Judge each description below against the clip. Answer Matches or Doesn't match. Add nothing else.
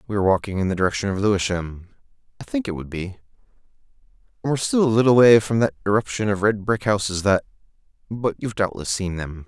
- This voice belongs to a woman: Doesn't match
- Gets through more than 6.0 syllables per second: Matches